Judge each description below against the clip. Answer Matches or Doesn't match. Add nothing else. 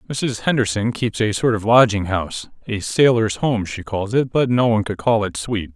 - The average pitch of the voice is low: Matches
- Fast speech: Matches